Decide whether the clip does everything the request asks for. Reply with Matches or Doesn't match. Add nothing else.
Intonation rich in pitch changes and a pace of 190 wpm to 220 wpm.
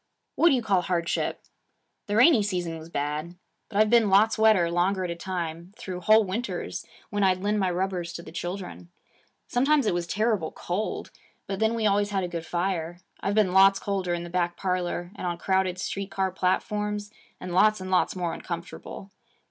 Doesn't match